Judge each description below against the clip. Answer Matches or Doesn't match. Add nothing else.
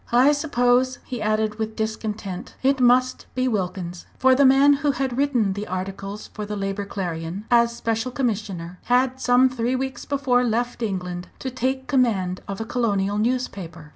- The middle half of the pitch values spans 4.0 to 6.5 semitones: Matches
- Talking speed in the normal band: Matches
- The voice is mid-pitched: Doesn't match